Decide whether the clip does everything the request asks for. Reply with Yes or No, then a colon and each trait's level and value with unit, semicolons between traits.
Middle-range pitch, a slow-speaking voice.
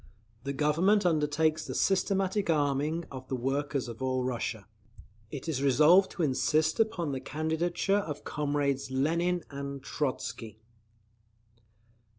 Yes: medium, 150 Hz; slow, 125 wpm